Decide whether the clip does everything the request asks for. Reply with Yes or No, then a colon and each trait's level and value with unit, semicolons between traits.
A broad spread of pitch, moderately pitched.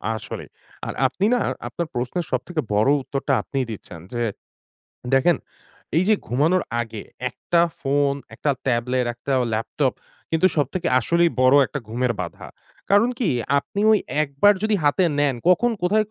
Yes: wide, 5.9 semitones; medium, 145 Hz